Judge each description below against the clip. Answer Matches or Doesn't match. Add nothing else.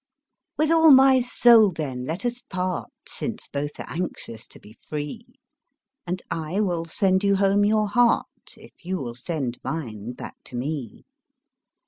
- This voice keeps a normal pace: Matches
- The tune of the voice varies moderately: Doesn't match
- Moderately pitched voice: Matches